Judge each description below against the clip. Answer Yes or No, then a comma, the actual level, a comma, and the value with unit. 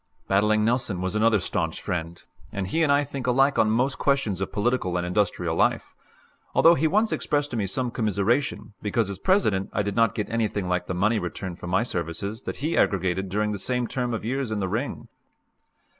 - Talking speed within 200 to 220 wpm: Yes, fast, 205 wpm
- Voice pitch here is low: Yes, low, 110 Hz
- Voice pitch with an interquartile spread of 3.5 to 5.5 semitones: Yes, average, 4.8 semitones